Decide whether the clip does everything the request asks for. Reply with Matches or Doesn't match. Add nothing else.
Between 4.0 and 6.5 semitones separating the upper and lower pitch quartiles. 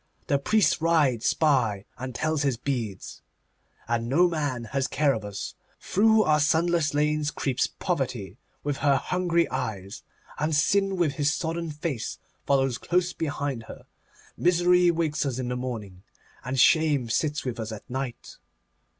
Matches